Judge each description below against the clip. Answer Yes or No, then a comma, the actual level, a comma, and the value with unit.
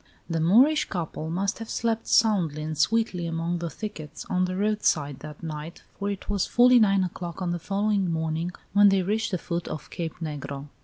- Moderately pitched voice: Yes, medium, 180 Hz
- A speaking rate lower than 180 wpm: No, average, 195 wpm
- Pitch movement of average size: Yes, average, 4.2 semitones